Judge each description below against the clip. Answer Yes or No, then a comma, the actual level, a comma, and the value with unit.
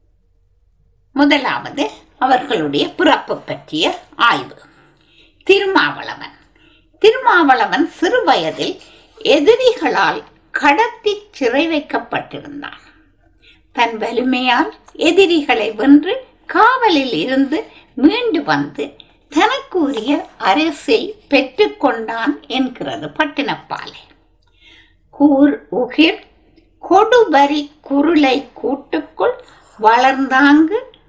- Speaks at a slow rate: Yes, slow, 60 wpm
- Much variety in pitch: Yes, wide, 7.4 semitones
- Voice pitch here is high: Yes, very high, 295 Hz